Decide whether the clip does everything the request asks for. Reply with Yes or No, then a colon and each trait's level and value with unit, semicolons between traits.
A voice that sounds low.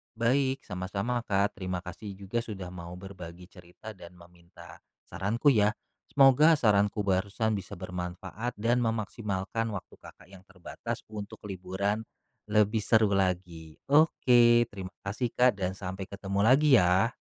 Yes: low, 100 Hz